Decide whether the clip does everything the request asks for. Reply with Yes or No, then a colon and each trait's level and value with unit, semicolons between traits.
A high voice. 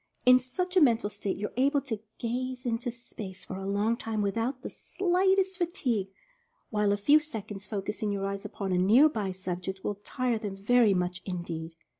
Yes: high, 220 Hz